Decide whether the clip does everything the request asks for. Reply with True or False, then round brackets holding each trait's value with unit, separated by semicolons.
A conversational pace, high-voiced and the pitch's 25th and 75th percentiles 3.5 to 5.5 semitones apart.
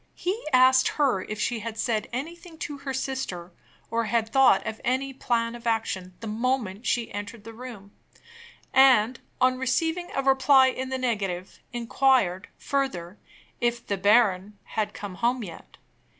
True (155 wpm; 240 Hz; 3.9 semitones)